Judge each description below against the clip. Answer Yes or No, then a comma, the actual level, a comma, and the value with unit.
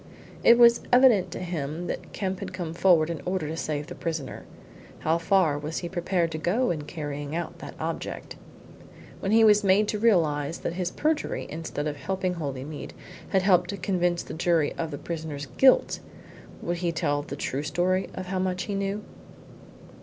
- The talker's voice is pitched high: No, medium, 175 Hz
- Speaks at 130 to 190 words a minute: Yes, average, 185 wpm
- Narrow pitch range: No, average, 3.6 semitones